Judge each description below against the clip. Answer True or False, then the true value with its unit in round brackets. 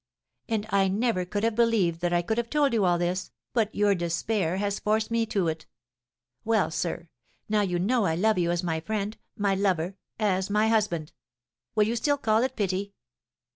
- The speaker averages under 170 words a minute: False (195 wpm)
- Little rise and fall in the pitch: False (3.7 semitones)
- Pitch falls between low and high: False (200 Hz)